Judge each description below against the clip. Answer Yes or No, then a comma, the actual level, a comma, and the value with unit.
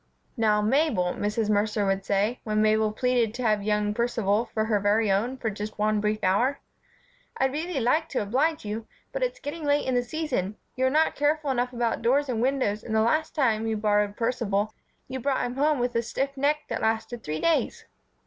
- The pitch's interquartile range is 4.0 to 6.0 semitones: Yes, average, 4.3 semitones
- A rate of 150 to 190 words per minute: No, fast, 205 wpm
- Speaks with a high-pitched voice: Yes, high, 230 Hz